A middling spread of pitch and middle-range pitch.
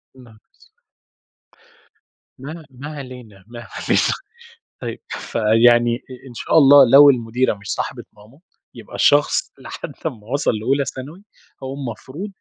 No: average, 3.4 semitones; low, 130 Hz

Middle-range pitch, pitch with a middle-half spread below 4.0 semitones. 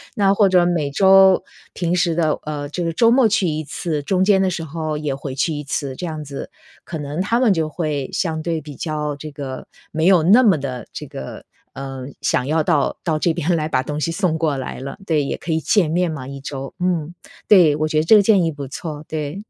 Yes: medium, 155 Hz; average, 3.5 semitones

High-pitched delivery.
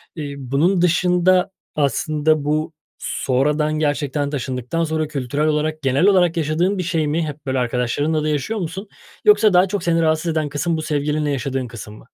No: medium, 155 Hz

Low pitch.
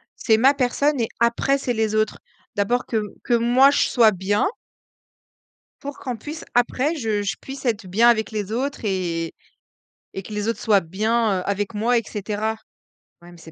No: high, 220 Hz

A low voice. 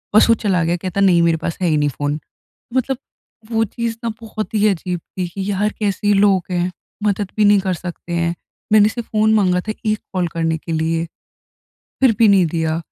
No: high, 190 Hz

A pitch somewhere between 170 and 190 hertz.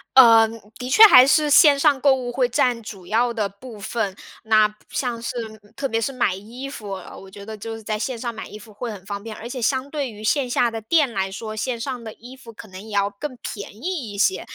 No: high, 230 Hz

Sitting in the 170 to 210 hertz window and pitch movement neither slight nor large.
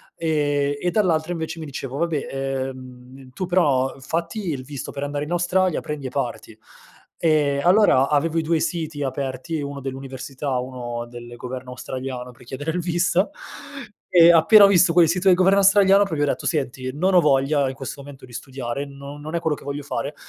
No: medium, 145 Hz; average, 4.1 semitones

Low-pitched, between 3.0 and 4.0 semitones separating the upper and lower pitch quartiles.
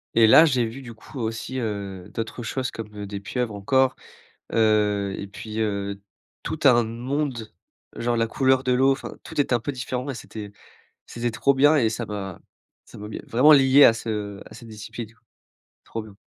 Yes: low, 115 Hz; average, 3.5 semitones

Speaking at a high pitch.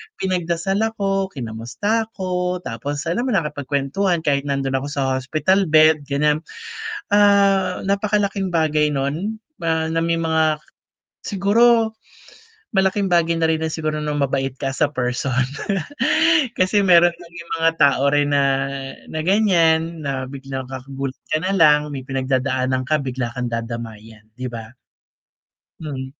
No: medium, 155 Hz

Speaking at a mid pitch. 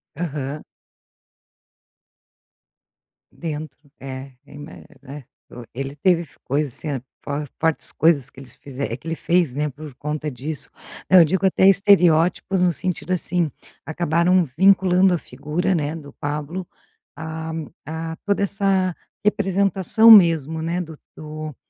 Yes: medium, 160 Hz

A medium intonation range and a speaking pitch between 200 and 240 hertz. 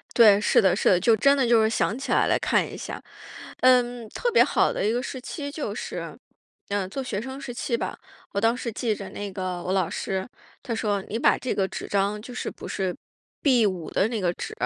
Yes: average, 4.0 semitones; high, 220 Hz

